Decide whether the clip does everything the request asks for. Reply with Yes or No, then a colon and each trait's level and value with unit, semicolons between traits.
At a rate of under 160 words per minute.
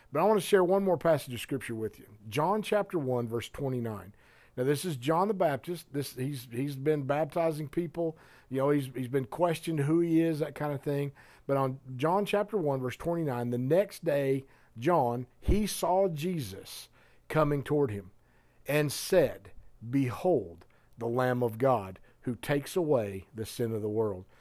No: average, 180 wpm